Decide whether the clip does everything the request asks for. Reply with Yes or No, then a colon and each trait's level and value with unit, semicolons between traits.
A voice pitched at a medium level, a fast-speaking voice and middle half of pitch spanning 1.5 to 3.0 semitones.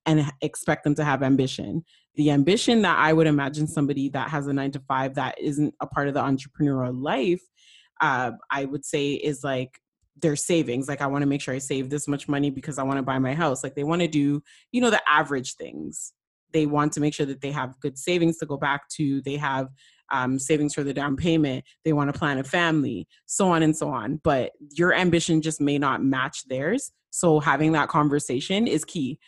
Yes: medium, 145 Hz; fast, 225 wpm; narrow, 2.4 semitones